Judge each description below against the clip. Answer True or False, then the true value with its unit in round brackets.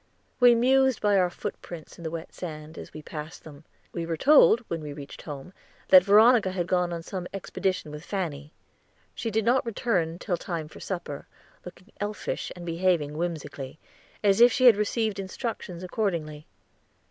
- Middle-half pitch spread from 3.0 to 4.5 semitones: False (4.9 semitones)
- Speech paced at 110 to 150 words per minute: False (170 wpm)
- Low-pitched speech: False (180 Hz)